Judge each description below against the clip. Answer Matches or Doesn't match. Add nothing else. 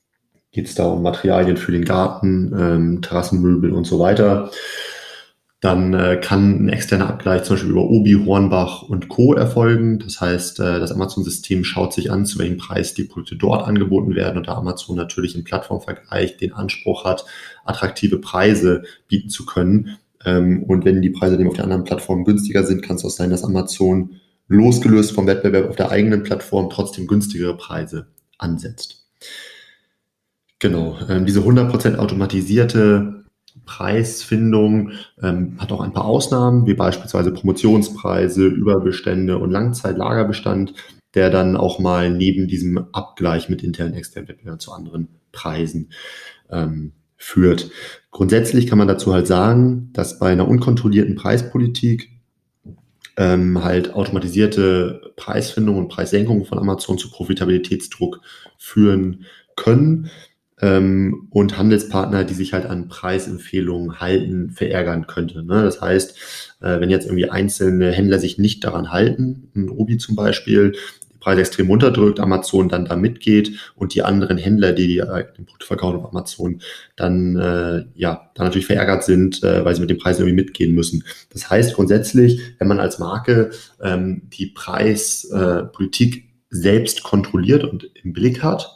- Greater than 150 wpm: Doesn't match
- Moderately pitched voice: Doesn't match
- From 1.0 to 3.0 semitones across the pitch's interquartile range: Matches